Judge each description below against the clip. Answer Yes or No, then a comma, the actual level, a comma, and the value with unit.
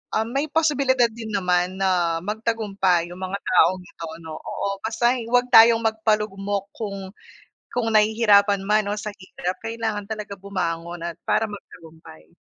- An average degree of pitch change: Yes, average, 3.3 semitones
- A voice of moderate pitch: No, high, 205 Hz